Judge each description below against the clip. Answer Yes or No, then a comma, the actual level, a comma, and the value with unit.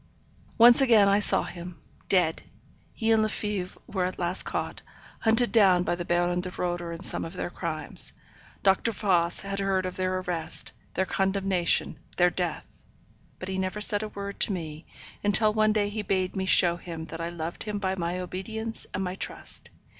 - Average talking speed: Yes, average, 185 wpm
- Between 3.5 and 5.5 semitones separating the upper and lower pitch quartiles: No, average, 2.8 semitones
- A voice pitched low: No, medium, 185 Hz